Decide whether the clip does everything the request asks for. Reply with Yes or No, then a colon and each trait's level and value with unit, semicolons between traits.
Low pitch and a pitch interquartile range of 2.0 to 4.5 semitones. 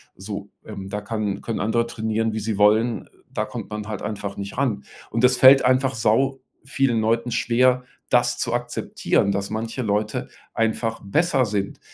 Yes: low, 115 Hz; average, 2.8 semitones